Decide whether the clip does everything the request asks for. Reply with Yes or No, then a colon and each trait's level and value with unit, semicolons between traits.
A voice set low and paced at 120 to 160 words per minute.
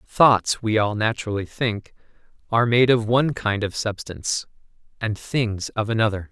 Yes: low, 110 Hz; average, 150 wpm